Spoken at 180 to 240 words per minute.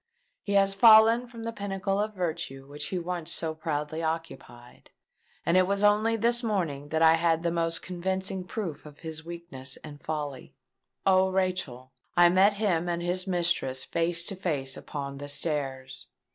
No: average, 165 wpm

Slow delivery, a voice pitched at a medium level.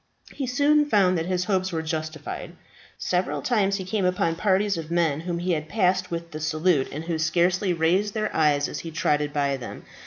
No: average, 195 wpm; medium, 175 Hz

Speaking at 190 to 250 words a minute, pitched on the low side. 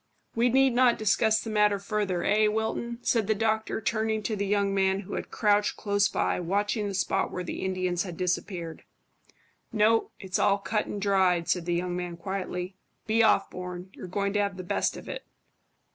No: average, 195 wpm; high, 200 Hz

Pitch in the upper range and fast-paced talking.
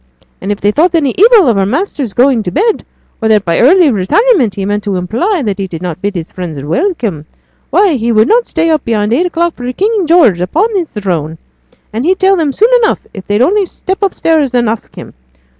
Yes: very high, 250 Hz; fast, 225 wpm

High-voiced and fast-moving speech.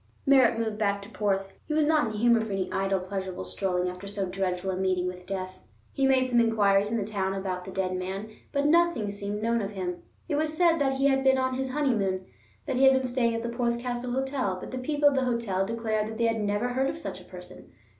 Yes: high, 225 Hz; fast, 250 wpm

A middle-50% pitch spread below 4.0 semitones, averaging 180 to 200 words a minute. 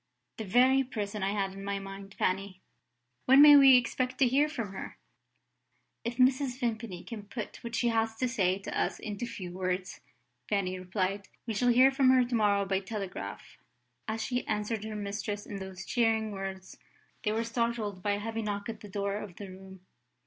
Yes: average, 3.4 semitones; average, 190 wpm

